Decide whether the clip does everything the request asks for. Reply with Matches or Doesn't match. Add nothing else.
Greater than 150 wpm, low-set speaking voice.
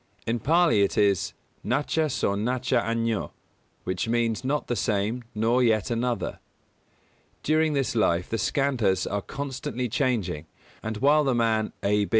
Doesn't match